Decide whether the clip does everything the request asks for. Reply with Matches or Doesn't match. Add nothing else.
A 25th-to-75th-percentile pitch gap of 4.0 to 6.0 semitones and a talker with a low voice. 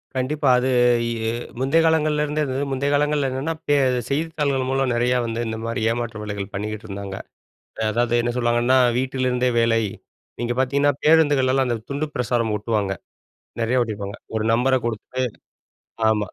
Doesn't match